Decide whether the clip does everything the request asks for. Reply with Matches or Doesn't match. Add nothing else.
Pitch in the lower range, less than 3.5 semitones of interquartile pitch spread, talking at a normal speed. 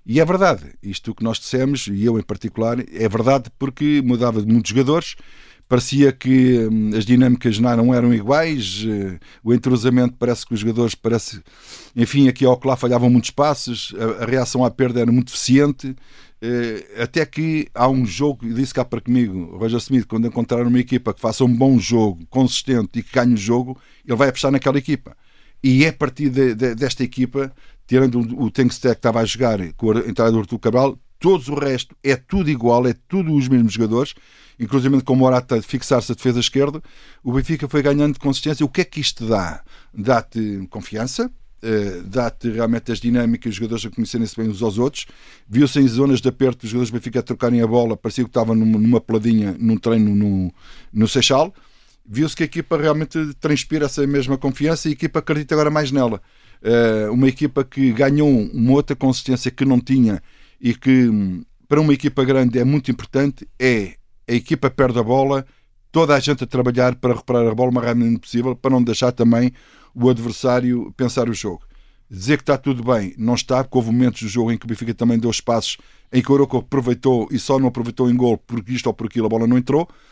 Doesn't match